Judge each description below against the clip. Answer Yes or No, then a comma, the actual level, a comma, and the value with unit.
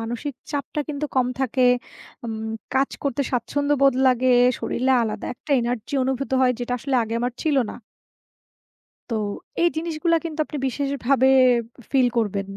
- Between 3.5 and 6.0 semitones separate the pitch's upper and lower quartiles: No, average, 3.0 semitones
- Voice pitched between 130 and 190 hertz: No, very high, 265 Hz